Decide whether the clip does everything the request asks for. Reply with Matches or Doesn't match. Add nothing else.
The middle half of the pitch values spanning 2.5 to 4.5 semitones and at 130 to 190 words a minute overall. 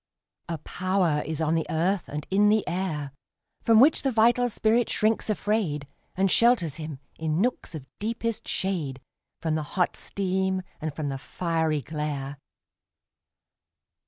Doesn't match